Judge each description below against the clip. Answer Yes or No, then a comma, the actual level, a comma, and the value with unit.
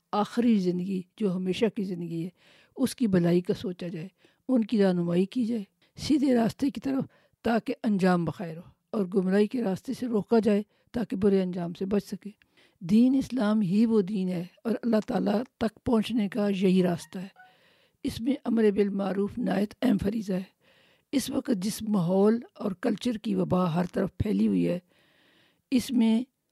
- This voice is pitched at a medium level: No, high, 210 Hz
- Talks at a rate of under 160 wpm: No, average, 175 wpm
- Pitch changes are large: No, average, 3.8 semitones